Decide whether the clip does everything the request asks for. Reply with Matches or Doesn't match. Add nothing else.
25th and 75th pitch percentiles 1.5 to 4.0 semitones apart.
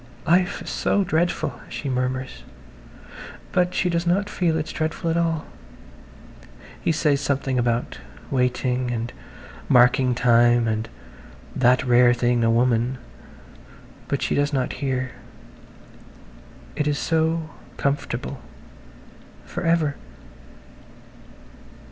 Doesn't match